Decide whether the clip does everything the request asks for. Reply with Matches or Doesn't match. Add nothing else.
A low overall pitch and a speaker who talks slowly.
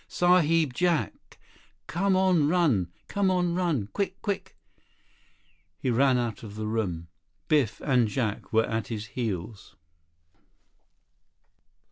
Matches